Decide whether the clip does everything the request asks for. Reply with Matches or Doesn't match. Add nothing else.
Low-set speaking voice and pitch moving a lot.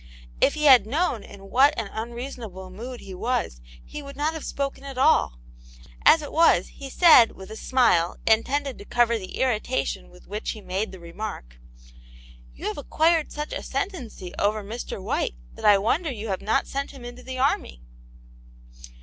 Doesn't match